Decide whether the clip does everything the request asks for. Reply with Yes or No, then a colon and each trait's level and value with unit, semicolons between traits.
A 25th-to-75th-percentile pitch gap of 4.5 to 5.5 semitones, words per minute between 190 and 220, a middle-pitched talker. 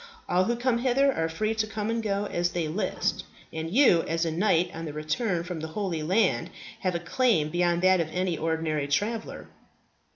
Yes: average, 4.9 semitones; average, 200 wpm; medium, 180 Hz